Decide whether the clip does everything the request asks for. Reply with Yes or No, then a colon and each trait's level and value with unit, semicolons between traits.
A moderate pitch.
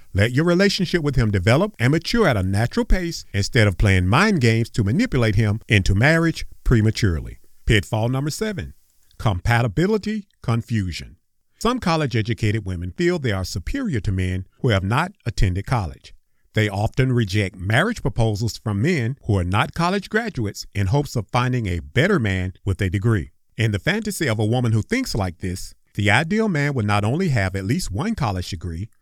No: low, 115 Hz